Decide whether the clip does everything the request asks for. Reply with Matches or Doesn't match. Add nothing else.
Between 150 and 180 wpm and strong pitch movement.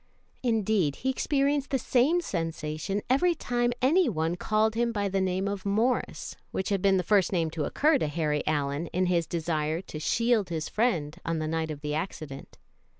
Doesn't match